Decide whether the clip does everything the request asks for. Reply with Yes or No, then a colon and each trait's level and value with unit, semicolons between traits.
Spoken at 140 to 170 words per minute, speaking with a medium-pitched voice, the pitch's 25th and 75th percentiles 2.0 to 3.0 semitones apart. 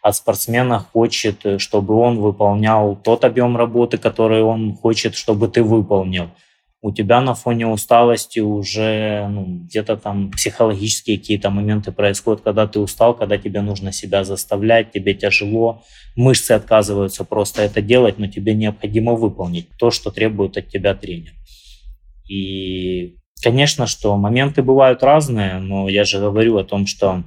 No: average, 145 wpm; low, 105 Hz; narrow, 2.4 semitones